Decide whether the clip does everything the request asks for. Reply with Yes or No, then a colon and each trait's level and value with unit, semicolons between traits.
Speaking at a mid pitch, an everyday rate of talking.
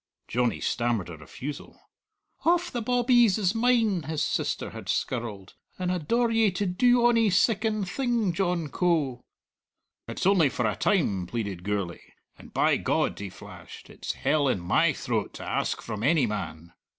Yes: medium, 170 Hz; average, 160 wpm